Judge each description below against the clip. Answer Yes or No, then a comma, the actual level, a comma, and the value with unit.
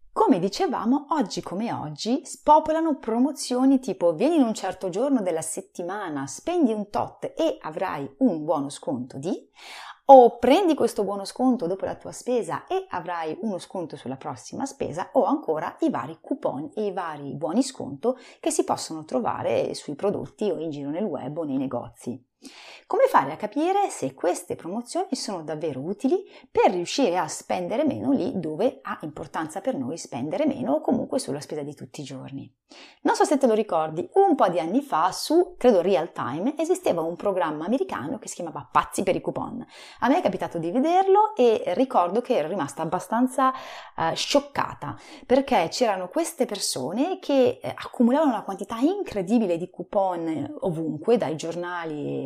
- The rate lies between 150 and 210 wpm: Yes, fast, 170 wpm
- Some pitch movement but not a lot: No, wide, 8.4 semitones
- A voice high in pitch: Yes, very high, 250 Hz